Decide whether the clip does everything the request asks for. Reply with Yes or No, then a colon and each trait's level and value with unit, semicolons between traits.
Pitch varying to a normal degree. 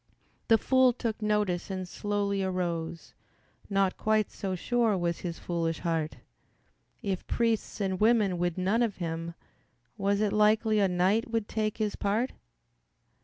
Yes: average, 3.4 semitones